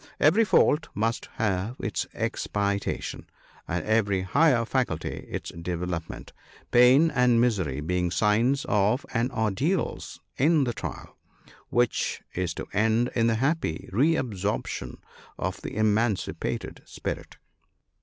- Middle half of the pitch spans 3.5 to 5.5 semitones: Yes, average, 4.8 semitones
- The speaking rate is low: Yes, slow, 125 wpm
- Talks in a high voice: No, low, 110 Hz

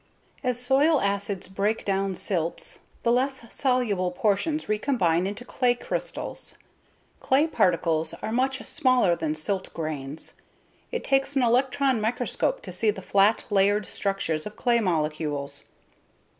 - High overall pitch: Yes, high, 210 Hz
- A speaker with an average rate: No, slow, 130 wpm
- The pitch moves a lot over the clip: Yes, wide, 6.1 semitones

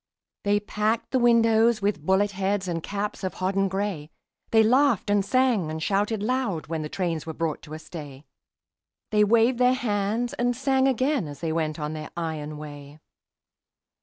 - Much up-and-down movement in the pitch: Yes, wide, 6.4 semitones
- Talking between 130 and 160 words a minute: No, average, 175 wpm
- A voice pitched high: Yes, high, 200 Hz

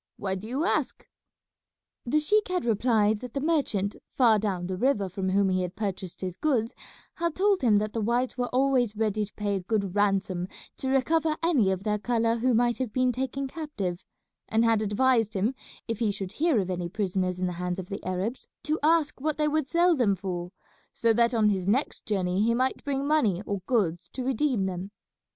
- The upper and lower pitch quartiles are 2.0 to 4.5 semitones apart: No, average, 5.3 semitones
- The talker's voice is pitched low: No, high, 220 Hz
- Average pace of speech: No, fast, 210 wpm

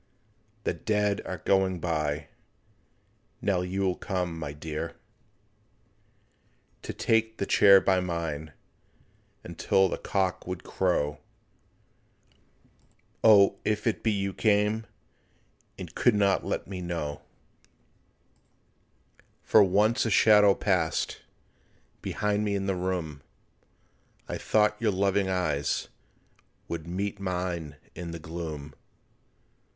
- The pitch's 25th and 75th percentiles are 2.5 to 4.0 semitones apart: Yes, average, 3.4 semitones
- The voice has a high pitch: No, very low, 95 Hz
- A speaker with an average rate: No, slow, 110 wpm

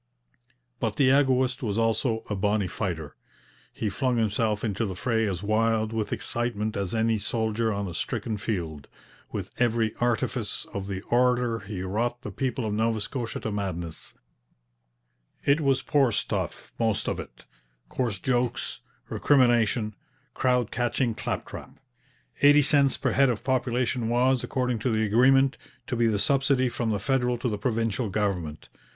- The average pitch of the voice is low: Yes, low, 115 Hz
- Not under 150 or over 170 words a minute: Yes, average, 155 wpm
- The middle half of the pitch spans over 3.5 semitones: No, average, 3.2 semitones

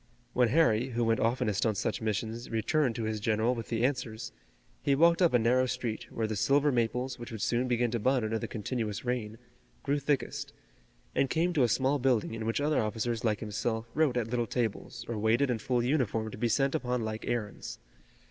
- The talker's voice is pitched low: Yes, low, 120 Hz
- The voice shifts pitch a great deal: No, narrow, 2.6 semitones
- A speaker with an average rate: No, fast, 210 wpm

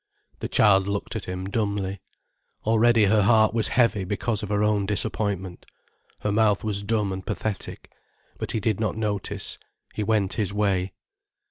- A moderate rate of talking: Yes, average, 160 wpm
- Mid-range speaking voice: No, low, 105 Hz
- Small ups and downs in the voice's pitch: Yes, narrow, 1.9 semitones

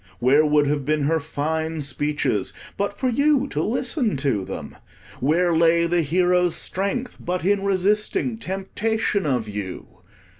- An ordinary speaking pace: Yes, average, 145 wpm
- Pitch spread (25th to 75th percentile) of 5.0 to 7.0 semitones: Yes, wide, 5.5 semitones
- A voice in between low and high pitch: Yes, medium, 170 Hz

